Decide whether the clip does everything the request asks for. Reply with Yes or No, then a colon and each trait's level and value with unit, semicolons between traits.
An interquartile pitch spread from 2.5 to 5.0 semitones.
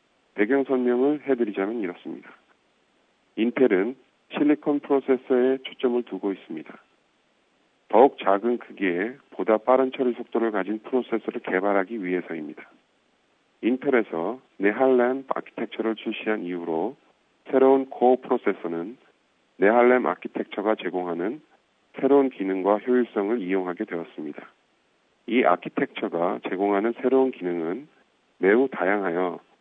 Yes: average, 4.7 semitones